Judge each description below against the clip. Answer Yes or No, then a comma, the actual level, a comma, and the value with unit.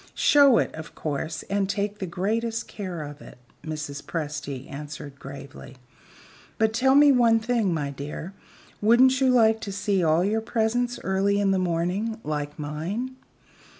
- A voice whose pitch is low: No, high, 195 Hz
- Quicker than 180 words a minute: No, average, 155 wpm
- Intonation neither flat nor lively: No, wide, 6.8 semitones